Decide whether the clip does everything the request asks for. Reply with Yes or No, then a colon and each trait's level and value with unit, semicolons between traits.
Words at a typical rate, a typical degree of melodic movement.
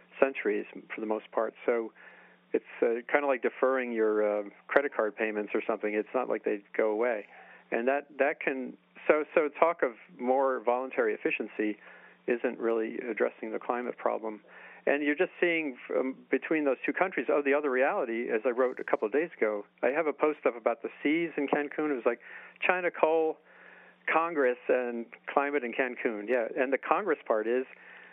Yes: average, 190 wpm; average, 4.8 semitones